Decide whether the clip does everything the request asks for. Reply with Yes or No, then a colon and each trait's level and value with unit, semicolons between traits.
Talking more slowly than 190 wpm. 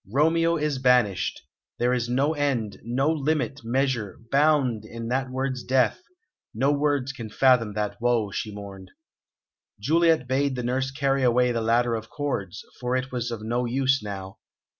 Yes: average, 160 wpm